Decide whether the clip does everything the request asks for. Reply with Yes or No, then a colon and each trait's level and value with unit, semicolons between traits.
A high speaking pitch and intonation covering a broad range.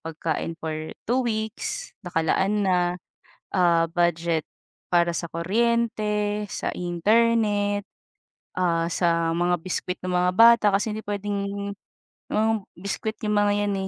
No: high, 200 Hz; average, 3.5 semitones